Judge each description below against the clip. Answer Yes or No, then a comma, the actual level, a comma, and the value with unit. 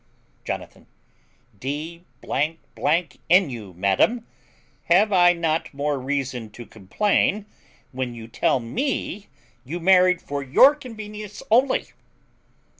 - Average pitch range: No, wide, 7.7 semitones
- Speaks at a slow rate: Yes, slow, 105 wpm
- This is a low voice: No, medium, 165 Hz